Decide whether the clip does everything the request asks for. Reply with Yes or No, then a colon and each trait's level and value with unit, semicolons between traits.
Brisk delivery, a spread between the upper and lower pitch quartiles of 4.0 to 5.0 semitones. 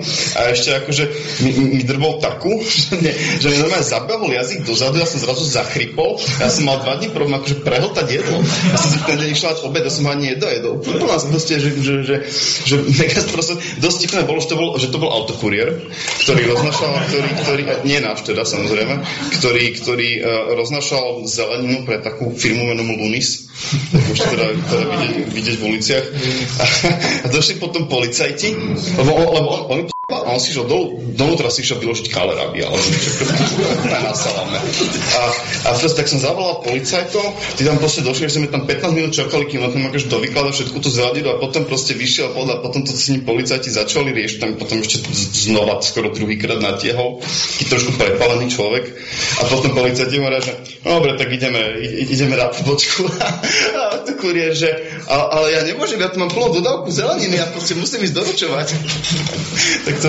Yes: fast, 185 wpm; average, 4.4 semitones